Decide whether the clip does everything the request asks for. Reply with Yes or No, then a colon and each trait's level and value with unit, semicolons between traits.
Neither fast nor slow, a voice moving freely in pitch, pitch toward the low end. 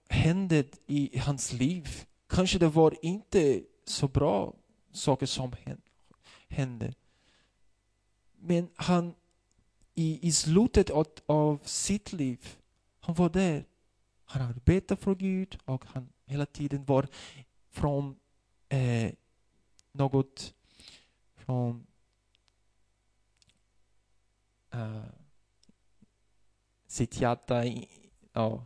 No: slow, 90 wpm; wide, 5.9 semitones; low, 130 Hz